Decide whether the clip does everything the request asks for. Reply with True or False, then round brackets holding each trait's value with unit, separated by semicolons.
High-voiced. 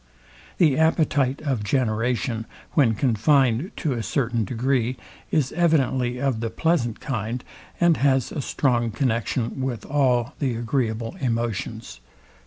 False (125 Hz)